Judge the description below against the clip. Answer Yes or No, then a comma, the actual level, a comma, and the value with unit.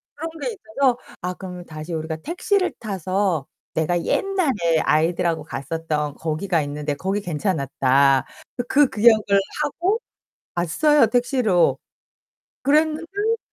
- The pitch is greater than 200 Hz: No, medium, 185 Hz